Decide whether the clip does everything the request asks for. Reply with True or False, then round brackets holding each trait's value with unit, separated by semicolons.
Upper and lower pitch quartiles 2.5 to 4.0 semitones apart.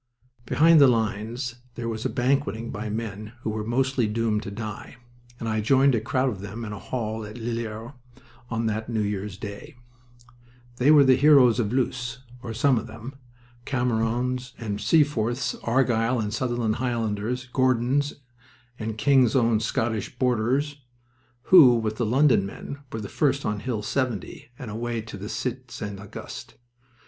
True (2.9 semitones)